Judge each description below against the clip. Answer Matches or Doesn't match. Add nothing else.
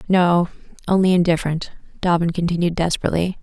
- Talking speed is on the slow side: Matches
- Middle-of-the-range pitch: Matches